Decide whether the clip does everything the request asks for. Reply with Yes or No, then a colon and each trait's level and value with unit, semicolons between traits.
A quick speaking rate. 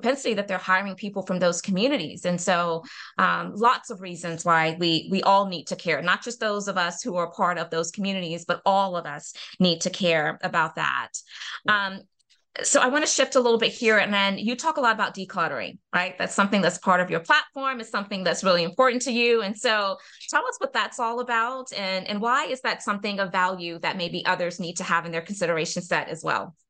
Yes: fast, 225 wpm